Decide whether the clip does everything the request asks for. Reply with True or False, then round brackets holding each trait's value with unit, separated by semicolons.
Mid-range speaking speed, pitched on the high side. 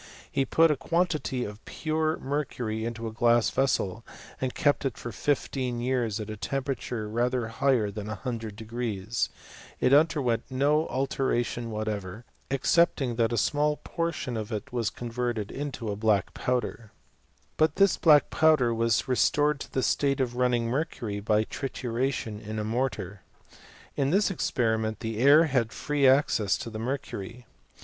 False (150 wpm; 120 Hz)